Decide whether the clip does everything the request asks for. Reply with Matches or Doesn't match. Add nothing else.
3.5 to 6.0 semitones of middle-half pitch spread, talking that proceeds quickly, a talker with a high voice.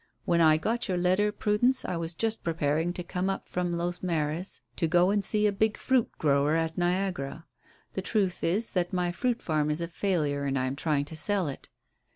Doesn't match